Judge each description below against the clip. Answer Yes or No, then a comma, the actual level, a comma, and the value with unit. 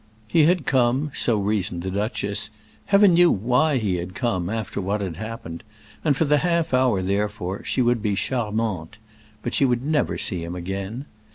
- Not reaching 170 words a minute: No, average, 175 wpm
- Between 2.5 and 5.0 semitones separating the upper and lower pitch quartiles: No, wide, 5.4 semitones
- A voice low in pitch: Yes, low, 110 Hz